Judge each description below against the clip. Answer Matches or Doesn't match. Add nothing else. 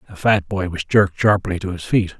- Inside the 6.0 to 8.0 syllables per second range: Doesn't match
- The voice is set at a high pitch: Doesn't match